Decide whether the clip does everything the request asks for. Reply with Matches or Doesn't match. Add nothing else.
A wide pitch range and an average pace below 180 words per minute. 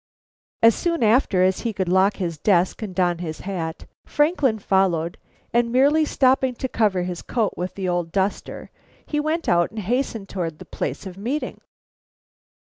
Matches